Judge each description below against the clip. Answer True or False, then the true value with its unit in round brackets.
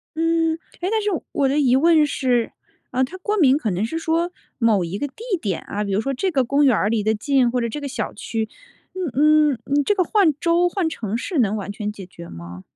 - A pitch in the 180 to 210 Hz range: False (265 Hz)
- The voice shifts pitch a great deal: True (6.9 semitones)